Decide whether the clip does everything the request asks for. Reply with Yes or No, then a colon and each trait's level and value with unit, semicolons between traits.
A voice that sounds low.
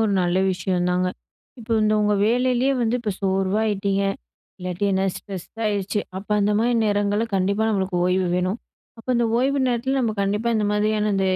No: high, 205 Hz